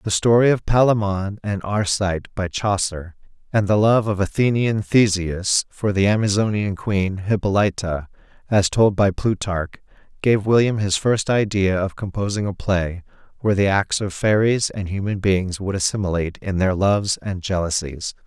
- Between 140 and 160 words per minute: Yes, average, 155 wpm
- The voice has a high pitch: No, low, 100 Hz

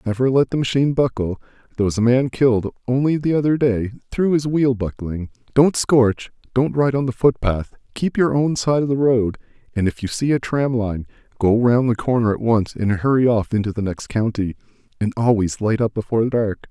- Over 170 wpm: Yes, average, 200 wpm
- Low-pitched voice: Yes, low, 120 Hz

